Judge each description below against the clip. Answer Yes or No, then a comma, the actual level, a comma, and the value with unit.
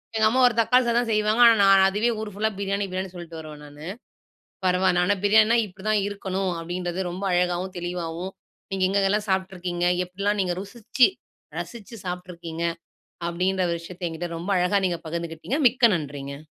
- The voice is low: No, medium, 185 Hz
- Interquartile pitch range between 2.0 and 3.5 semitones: Yes, average, 2.9 semitones